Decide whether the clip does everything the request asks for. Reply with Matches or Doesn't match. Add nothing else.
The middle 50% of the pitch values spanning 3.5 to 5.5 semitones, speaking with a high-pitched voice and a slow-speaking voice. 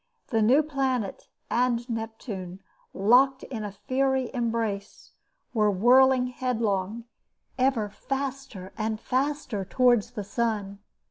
Matches